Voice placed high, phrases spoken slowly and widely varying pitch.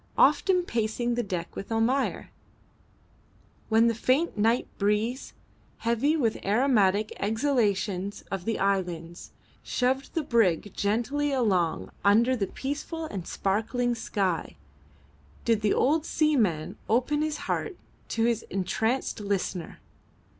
No: high, 225 Hz; slow, 120 wpm; average, 4.6 semitones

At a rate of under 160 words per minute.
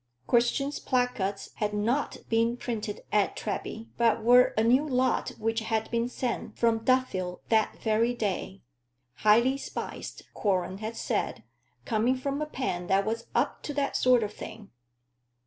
Yes: average, 150 wpm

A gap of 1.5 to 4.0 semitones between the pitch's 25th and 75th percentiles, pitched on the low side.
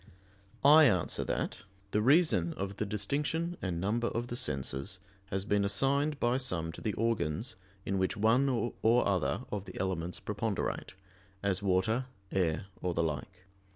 No: average, 4.8 semitones; low, 100 Hz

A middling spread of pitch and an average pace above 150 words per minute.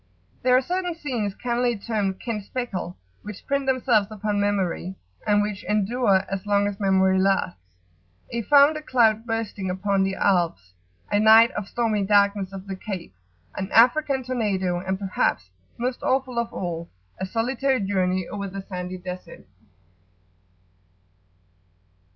No: average, 3.9 semitones; average, 140 wpm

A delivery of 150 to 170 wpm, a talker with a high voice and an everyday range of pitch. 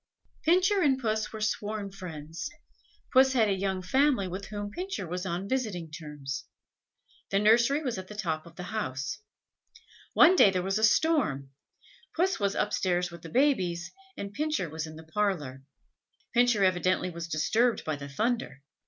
No: average, 165 wpm; high, 195 Hz; wide, 5.7 semitones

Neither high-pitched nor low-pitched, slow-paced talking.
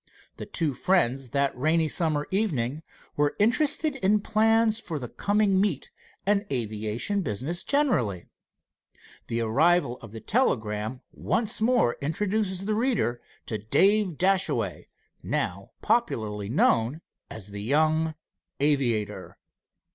Yes: medium, 155 Hz; slow, 115 wpm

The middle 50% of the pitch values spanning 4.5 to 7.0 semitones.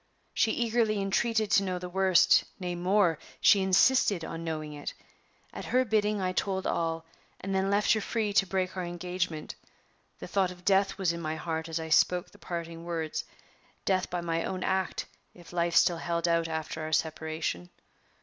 No: average, 2.9 semitones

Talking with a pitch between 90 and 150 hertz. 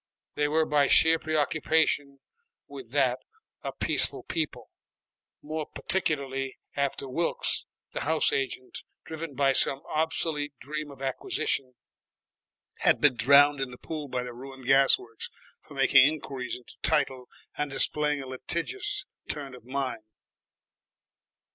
Yes: medium, 140 Hz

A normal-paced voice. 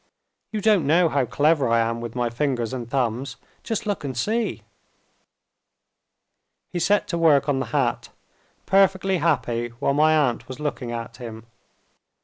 Yes: average, 155 wpm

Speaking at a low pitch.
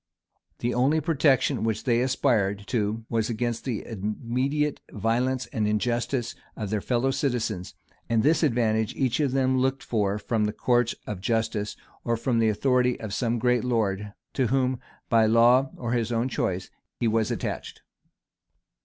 Yes: low, 120 Hz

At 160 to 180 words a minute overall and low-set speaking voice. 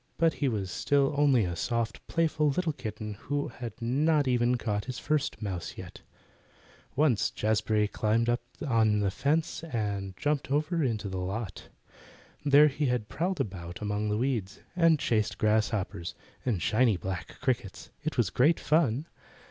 Yes: average, 165 wpm; low, 120 Hz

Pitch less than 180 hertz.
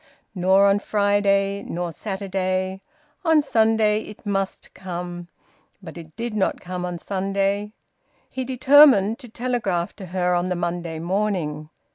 No: high, 195 Hz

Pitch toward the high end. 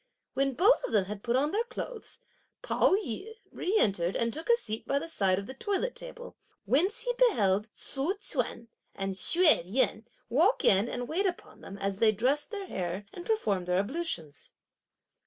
Yes: very high, 260 Hz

